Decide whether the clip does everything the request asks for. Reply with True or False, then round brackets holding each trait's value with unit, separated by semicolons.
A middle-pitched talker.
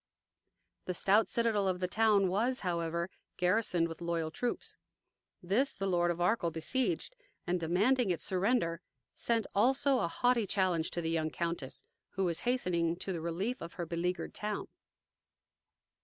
True (180 Hz)